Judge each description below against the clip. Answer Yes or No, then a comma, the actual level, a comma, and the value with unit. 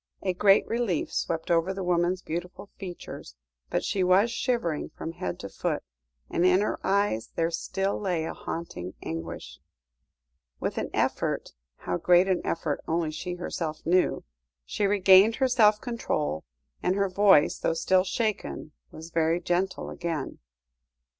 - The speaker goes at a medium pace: Yes, average, 150 wpm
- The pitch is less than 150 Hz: No, medium, 180 Hz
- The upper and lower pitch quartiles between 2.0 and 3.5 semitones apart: Yes, average, 3.1 semitones